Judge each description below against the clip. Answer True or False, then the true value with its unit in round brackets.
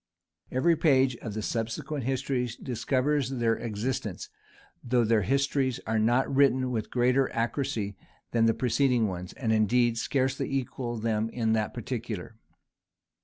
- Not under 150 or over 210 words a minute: False (135 wpm)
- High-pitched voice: False (120 Hz)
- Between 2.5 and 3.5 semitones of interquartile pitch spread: True (2.9 semitones)